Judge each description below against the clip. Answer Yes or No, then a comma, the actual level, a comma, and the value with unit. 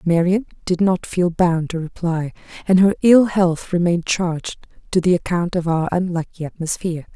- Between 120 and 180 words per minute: Yes, average, 170 wpm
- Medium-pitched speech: Yes, medium, 175 Hz